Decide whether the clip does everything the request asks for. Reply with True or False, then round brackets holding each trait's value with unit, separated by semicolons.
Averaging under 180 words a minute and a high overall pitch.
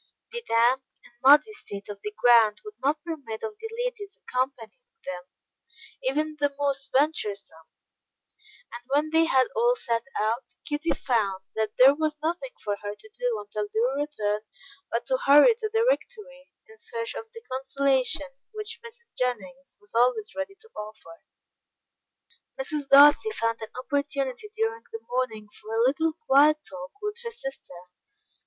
True (160 wpm; 275 Hz)